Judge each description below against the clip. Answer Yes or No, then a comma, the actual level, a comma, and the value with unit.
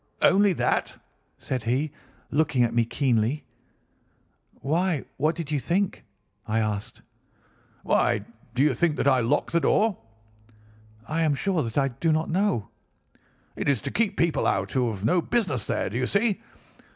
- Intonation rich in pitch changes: Yes, wide, 6.1 semitones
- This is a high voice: No, medium, 145 Hz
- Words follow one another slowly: No, average, 165 wpm